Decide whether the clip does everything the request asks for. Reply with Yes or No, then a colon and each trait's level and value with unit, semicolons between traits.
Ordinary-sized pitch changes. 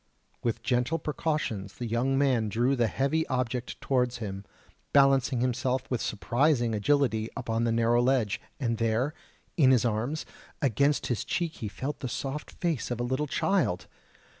Yes: average, 3.3 semitones